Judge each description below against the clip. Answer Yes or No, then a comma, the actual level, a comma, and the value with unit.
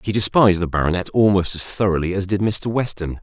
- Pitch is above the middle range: No, very low, 95 Hz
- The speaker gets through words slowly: No, fast, 205 wpm